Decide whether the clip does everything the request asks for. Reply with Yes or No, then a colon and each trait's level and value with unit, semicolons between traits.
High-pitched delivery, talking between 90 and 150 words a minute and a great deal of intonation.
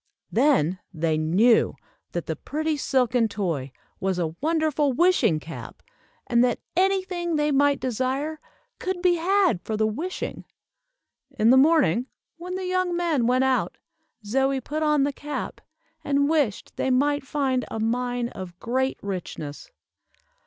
Yes: very high, 265 Hz; average, 145 wpm; wide, 6.0 semitones